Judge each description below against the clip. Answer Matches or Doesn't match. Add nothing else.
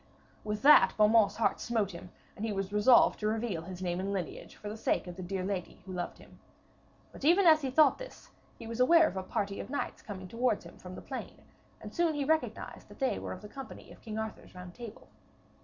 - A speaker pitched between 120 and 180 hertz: Doesn't match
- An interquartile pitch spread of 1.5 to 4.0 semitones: Doesn't match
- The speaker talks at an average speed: Doesn't match